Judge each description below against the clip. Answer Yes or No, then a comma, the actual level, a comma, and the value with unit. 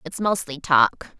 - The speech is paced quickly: No, average, 150 wpm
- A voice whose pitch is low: No, medium, 160 Hz